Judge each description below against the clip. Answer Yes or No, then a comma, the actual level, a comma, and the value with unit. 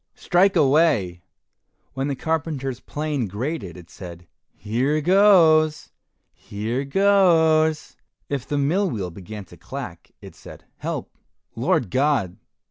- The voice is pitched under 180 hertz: Yes, medium, 140 Hz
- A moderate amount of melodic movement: No, wide, 6.9 semitones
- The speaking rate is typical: No, slow, 120 wpm